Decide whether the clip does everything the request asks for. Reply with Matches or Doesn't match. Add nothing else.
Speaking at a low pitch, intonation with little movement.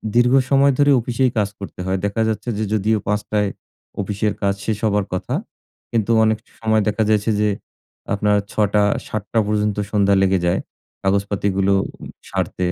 Matches